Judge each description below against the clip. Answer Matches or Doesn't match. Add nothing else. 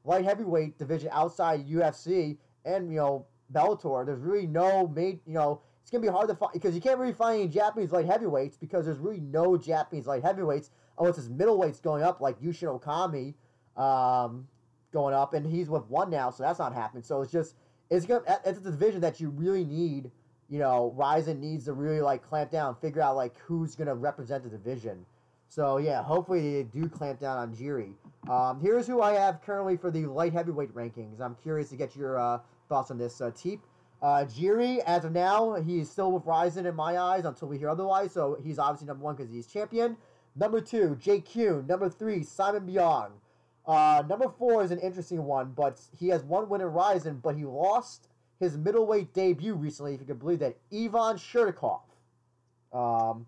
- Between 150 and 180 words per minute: Doesn't match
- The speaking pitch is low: Doesn't match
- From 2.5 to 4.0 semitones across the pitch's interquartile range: Doesn't match